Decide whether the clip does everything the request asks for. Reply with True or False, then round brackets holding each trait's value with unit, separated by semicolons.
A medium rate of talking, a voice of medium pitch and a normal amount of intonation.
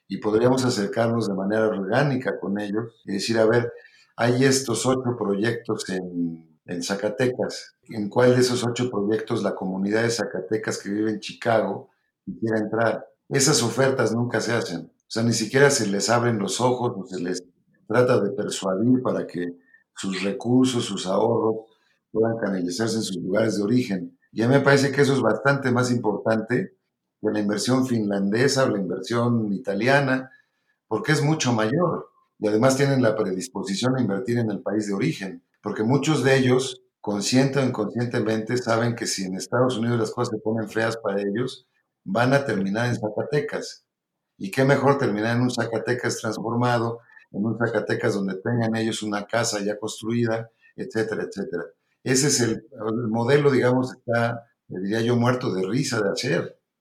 False (170 wpm; 115 Hz; 3.0 semitones)